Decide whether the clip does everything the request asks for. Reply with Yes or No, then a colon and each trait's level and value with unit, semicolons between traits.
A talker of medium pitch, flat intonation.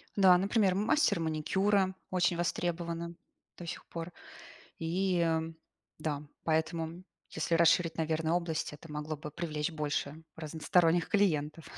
Yes: medium, 165 Hz; narrow, 2.0 semitones